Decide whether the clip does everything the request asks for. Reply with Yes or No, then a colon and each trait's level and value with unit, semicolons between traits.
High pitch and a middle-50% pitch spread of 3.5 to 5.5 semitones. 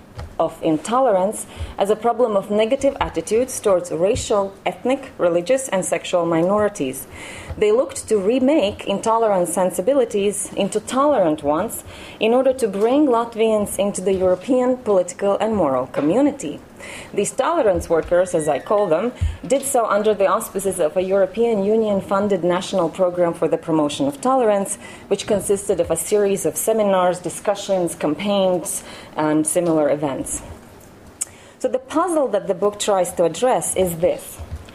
Yes: high, 195 Hz; average, 4.6 semitones